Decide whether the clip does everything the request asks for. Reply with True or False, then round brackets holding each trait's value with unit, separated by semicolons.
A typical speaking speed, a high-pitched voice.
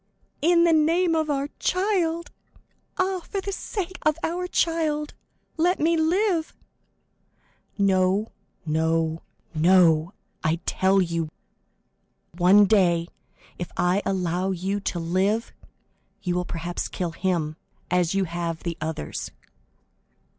False (120 wpm; 195 Hz)